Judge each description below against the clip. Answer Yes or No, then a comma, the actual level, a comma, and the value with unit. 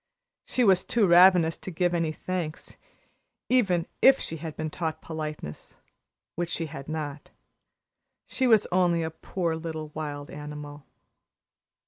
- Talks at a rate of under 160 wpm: Yes, slow, 135 wpm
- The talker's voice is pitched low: No, medium, 165 Hz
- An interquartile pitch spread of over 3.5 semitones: No, average, 2.8 semitones